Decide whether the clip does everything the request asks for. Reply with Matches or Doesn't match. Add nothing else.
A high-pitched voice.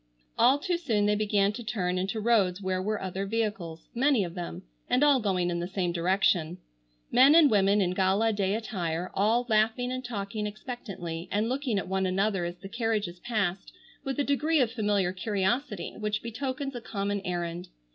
Matches